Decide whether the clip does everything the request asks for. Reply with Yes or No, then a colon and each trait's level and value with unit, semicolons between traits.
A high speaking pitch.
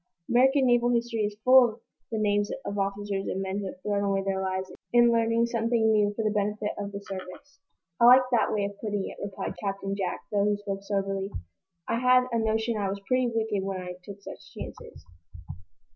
Yes: high, 205 Hz